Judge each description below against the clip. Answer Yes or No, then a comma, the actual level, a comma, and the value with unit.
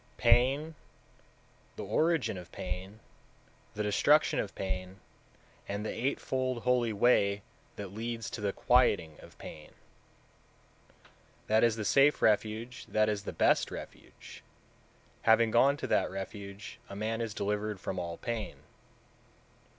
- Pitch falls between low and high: No, low, 110 Hz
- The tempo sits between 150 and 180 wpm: No, slow, 135 wpm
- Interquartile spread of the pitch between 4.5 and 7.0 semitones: No, average, 3.4 semitones